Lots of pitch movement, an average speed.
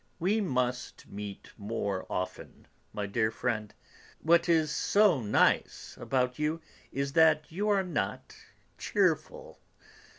No: wide, 7.7 semitones; slow, 120 wpm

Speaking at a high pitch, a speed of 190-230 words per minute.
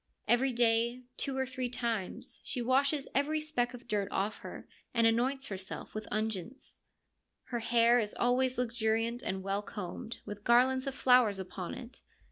No: high, 235 Hz; average, 160 wpm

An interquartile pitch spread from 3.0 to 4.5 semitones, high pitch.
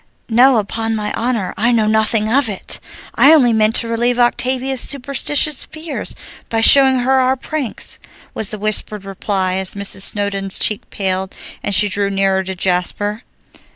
Yes: average, 4.1 semitones; high, 220 Hz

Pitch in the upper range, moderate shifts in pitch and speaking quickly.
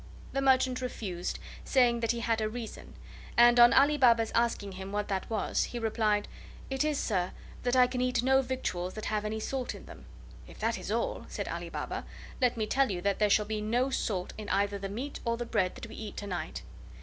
Yes: high, 230 Hz; average, 3.5 semitones; fast, 225 wpm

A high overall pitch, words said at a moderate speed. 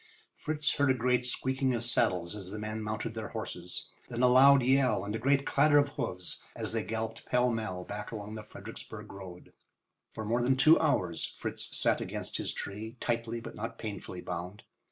No: low, 115 Hz; average, 195 wpm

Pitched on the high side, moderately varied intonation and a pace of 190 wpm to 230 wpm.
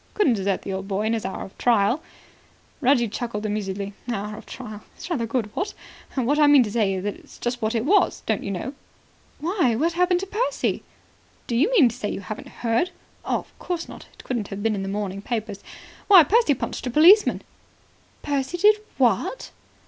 No: high, 235 Hz; wide, 7.0 semitones; average, 200 wpm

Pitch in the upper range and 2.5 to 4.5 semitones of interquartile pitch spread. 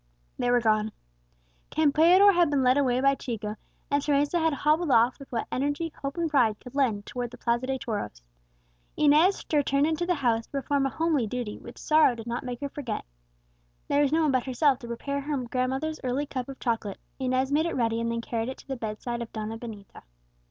Yes: very high, 260 Hz; average, 3.6 semitones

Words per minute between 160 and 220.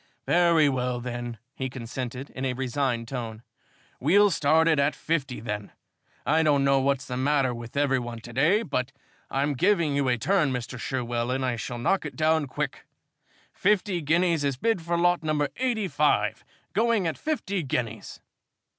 Yes: average, 170 wpm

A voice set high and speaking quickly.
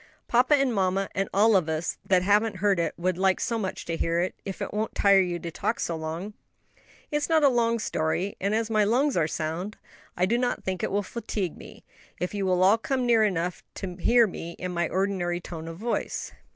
Yes: high, 195 Hz; fast, 230 wpm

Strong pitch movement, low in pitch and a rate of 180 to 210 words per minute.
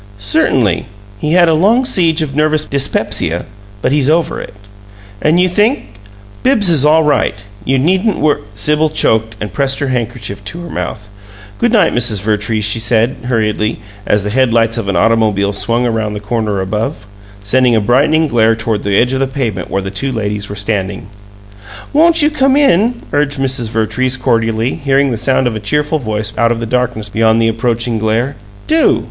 Yes: wide, 5.7 semitones; low, 120 Hz; average, 190 wpm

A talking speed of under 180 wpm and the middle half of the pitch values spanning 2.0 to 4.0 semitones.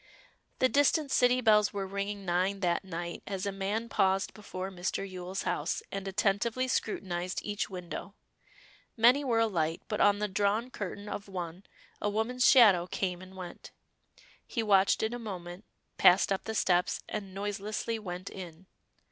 Yes: average, 160 wpm; average, 2.8 semitones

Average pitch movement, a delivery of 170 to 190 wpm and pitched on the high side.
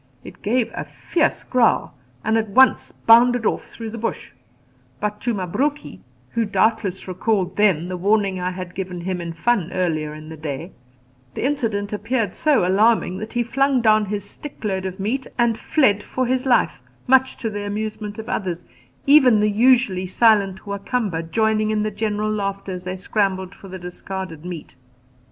Yes: average, 3.7 semitones; average, 180 wpm; high, 210 Hz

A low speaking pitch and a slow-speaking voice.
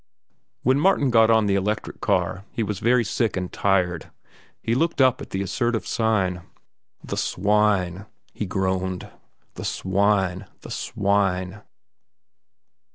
Yes: low, 100 Hz; slow, 130 wpm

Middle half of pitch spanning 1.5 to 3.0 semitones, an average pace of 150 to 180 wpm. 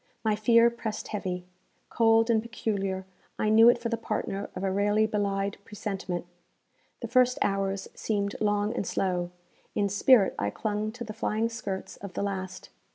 Yes: narrow, 2.4 semitones; average, 165 wpm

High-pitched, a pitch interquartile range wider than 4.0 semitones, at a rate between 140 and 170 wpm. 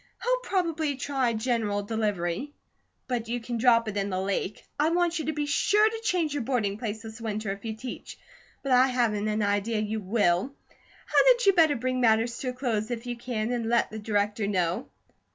No: high, 230 Hz; average, 4.4 semitones; fast, 205 wpm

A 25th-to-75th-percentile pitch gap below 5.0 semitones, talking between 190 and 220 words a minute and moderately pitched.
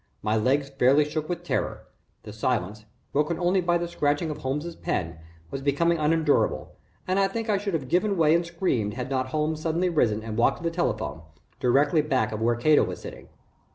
No: average, 5.3 semitones; average, 200 wpm; medium, 150 Hz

